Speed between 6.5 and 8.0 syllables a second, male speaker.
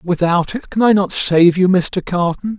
No: 4.3 syllables/s; male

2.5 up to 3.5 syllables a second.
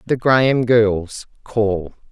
Yes: 3.0 syllables/s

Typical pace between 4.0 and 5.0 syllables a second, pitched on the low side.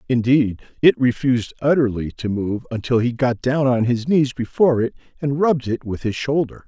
No: 5.3 syllables/s; low, 125 Hz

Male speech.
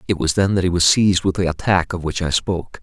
Yes: male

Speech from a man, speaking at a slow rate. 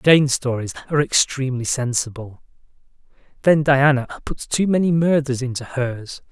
Yes: male; slow, 125 wpm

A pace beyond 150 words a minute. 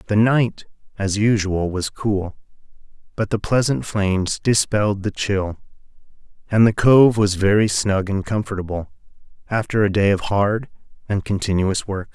No: average, 145 wpm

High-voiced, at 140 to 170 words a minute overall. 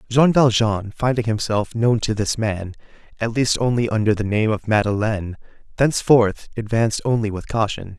No: low, 110 Hz; average, 160 wpm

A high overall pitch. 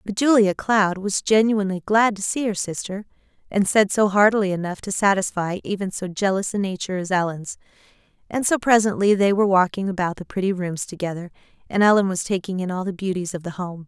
Yes: high, 195 Hz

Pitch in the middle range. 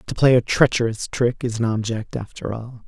No: low, 115 Hz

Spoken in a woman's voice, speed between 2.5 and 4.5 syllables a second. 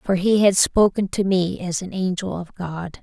Yes: female; 4.4 syllables/s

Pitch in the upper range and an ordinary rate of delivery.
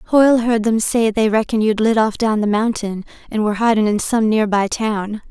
No: high, 220 Hz; fast, 225 wpm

